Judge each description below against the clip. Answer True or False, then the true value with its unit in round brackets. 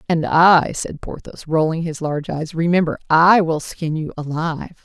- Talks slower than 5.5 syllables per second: True (4.7 syllables/s)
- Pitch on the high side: False (160 Hz)